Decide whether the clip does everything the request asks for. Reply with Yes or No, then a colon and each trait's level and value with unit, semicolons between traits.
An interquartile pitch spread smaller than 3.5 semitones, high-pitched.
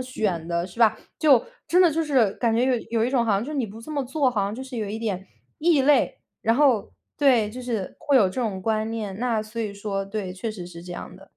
No: average, 4.3 semitones; high, 225 Hz